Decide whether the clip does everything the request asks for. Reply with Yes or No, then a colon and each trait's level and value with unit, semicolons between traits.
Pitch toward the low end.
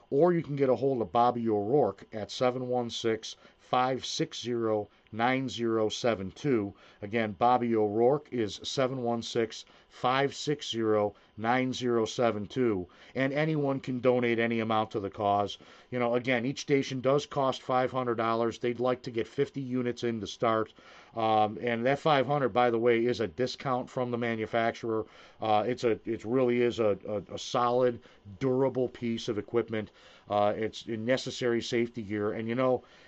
Yes: low, 120 Hz